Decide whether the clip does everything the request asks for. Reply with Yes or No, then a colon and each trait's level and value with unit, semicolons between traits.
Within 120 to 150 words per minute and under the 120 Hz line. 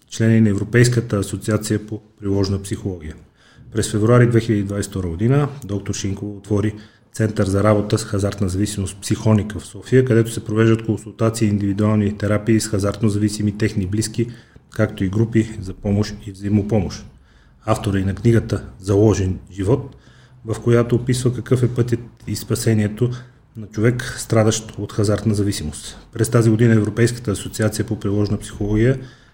Yes: average, 145 wpm; low, 110 Hz